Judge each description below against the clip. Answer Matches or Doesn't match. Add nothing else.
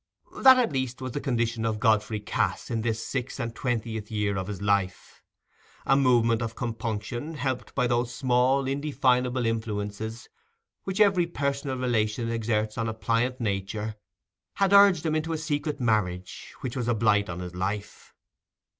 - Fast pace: Doesn't match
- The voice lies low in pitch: Matches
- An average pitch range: Matches